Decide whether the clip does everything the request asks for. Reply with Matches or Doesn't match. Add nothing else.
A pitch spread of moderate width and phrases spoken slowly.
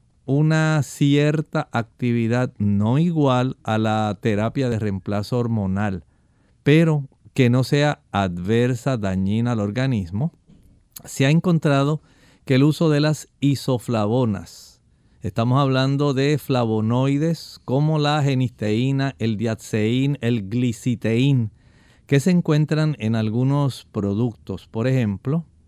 Matches